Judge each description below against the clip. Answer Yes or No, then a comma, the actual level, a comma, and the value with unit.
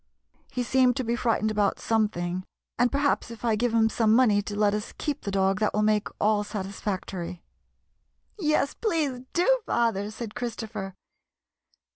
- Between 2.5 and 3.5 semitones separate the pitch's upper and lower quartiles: Yes, average, 3.1 semitones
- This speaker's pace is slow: No, average, 160 wpm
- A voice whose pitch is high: Yes, high, 220 Hz